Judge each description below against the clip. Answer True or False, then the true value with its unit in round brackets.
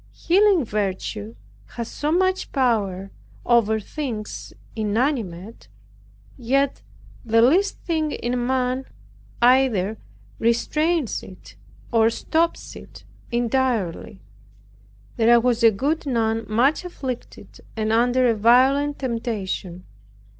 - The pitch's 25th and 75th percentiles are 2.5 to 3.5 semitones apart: False (3.9 semitones)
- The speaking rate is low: True (100 wpm)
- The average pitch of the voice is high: True (240 Hz)